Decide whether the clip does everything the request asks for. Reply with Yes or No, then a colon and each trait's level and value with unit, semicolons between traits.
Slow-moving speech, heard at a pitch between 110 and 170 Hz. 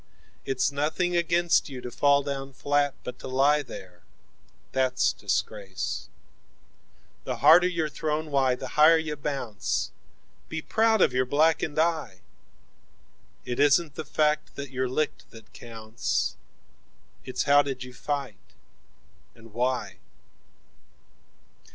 Yes: slow, 120 wpm; medium, 140 Hz